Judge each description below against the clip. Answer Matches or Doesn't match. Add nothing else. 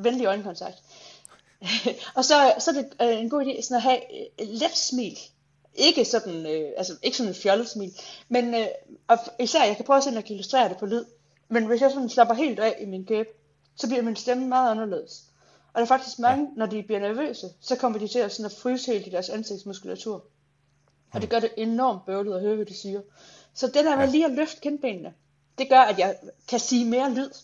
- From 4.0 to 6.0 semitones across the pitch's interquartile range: Matches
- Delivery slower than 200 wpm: Doesn't match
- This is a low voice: Doesn't match